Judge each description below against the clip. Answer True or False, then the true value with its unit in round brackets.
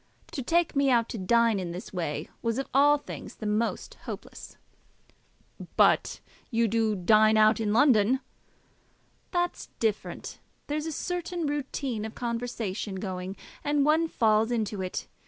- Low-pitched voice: False (230 Hz)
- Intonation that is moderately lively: True (5.0 semitones)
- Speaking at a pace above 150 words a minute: False (145 wpm)